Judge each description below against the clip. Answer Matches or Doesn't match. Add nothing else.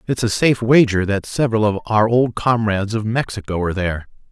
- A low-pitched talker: Matches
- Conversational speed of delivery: Matches